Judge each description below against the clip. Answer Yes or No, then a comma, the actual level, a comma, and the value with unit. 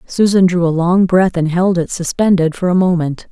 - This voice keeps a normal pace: No, fast, 215 wpm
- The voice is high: No, medium, 175 Hz